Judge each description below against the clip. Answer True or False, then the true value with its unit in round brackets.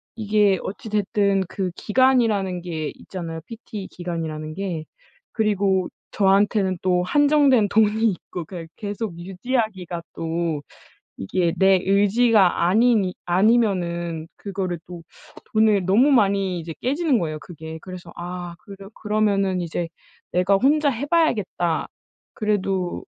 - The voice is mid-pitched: False (195 Hz)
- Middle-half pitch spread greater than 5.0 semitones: False (3.6 semitones)